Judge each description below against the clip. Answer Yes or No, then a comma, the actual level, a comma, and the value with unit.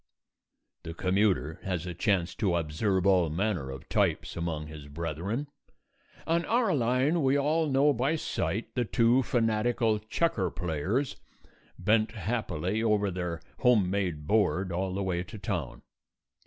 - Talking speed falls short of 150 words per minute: Yes, average, 140 wpm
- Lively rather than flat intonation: Yes, wide, 5.7 semitones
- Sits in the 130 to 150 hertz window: No, low, 100 Hz